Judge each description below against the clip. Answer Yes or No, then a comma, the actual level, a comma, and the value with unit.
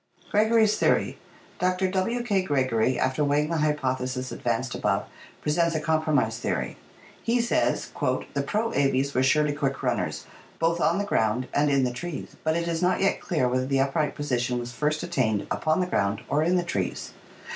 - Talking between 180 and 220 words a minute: Yes, average, 185 wpm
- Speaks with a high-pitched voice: No, medium, 150 Hz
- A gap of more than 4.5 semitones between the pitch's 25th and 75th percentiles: Yes, average, 5.2 semitones